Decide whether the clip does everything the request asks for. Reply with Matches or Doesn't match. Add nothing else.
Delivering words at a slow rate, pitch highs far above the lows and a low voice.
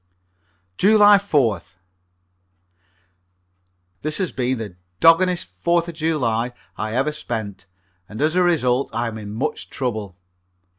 Matches